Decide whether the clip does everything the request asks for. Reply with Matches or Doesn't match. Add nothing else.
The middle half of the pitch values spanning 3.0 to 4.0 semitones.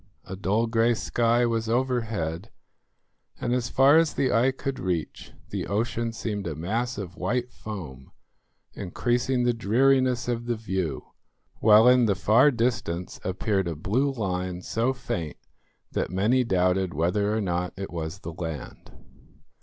Doesn't match